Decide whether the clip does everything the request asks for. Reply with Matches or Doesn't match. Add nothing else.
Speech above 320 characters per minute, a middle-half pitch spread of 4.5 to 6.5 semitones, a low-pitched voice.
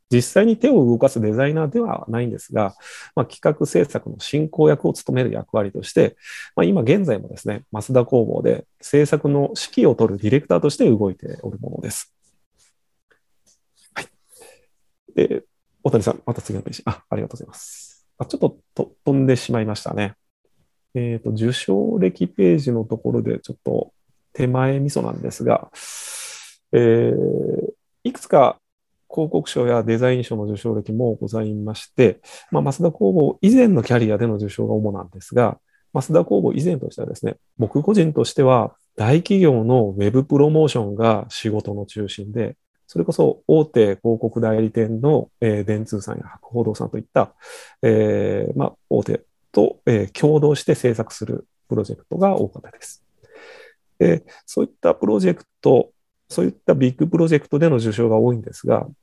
Matches